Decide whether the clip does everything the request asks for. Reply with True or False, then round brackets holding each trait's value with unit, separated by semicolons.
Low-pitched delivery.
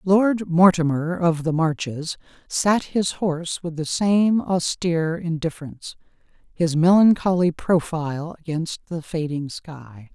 False (170 Hz)